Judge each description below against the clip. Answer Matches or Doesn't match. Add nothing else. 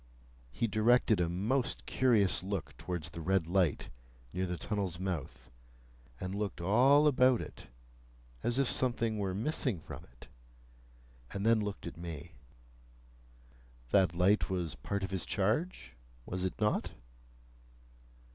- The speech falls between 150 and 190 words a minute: Doesn't match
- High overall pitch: Doesn't match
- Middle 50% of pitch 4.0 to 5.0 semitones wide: Matches